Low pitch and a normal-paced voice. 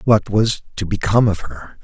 Yes: low, 105 Hz; average, 195 wpm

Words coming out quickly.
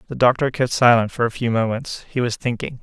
Yes: fast, 235 wpm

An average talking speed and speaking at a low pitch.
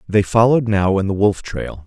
No: fast, 225 wpm; low, 105 Hz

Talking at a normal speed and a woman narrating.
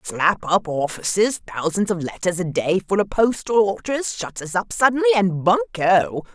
Yes: average, 150 wpm; female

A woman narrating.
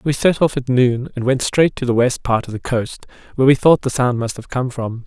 No: male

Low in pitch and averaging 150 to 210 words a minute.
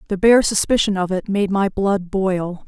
No: high, 195 Hz; average, 200 wpm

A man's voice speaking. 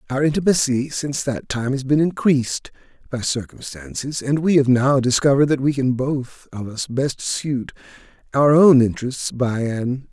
Yes: male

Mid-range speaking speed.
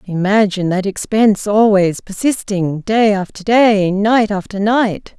No: slow, 125 wpm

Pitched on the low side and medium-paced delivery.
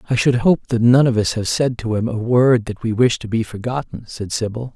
No: low, 115 Hz; fast, 265 wpm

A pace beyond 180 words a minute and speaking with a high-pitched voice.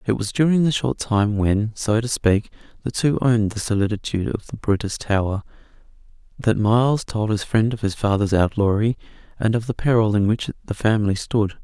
No: average, 190 wpm; low, 110 Hz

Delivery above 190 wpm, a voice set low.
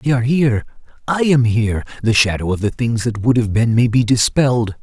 Yes: average, 200 wpm; low, 120 Hz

